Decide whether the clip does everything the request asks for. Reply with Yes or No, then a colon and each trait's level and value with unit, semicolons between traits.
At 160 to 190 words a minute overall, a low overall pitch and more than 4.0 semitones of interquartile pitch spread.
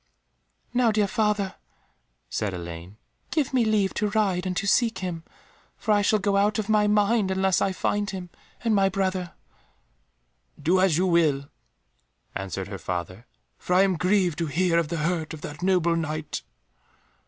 No: average, 170 wpm; medium, 185 Hz; average, 4.4 semitones